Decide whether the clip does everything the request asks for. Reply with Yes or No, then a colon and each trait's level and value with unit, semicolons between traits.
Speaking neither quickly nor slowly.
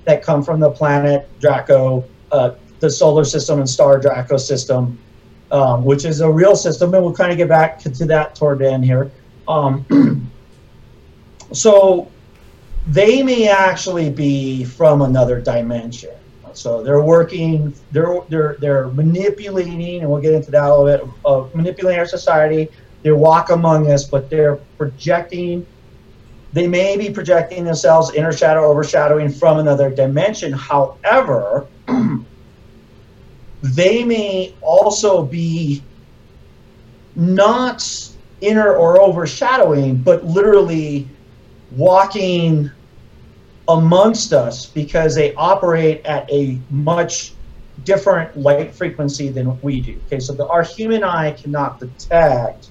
No: slow, 130 wpm